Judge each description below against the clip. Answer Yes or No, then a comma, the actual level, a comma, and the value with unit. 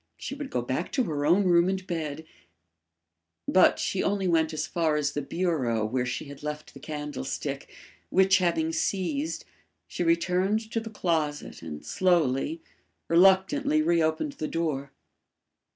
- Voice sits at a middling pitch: Yes, medium, 170 Hz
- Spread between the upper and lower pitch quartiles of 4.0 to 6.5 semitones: Yes, average, 4.4 semitones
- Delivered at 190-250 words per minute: No, average, 150 wpm